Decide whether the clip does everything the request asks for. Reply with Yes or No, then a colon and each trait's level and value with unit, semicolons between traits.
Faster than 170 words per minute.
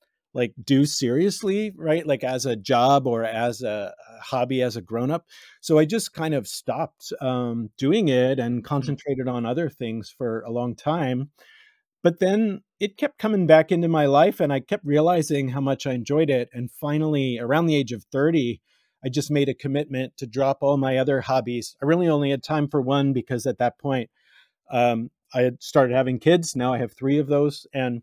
Yes: average, 200 wpm